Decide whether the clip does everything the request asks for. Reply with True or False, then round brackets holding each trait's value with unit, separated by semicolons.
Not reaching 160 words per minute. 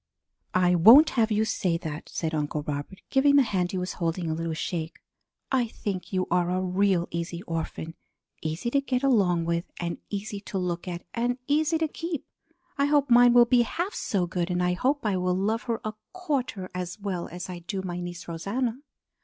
False (205 wpm)